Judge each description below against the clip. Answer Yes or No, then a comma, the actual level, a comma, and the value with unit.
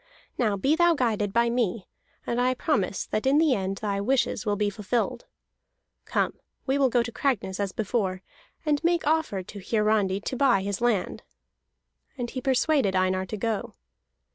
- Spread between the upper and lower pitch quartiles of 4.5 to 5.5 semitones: Yes, average, 4.9 semitones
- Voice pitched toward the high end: Yes, high, 225 Hz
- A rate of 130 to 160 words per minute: No, average, 170 wpm